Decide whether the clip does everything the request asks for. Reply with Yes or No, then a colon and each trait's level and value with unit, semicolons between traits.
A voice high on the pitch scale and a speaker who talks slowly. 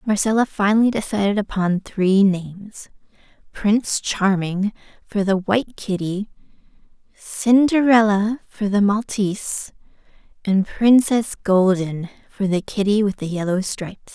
Yes: high, 205 Hz; slow, 110 wpm